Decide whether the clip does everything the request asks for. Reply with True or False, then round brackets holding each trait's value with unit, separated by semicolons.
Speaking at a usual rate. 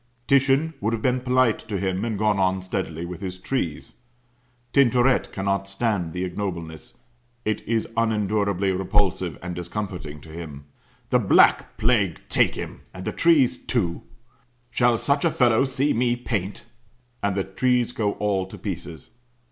True (155 wpm)